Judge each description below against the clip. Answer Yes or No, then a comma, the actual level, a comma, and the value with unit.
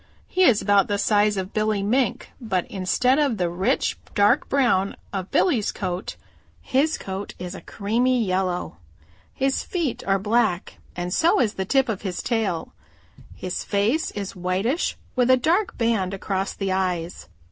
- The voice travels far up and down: No, average, 4.8 semitones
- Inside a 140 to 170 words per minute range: Yes, average, 160 wpm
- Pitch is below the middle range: No, high, 205 Hz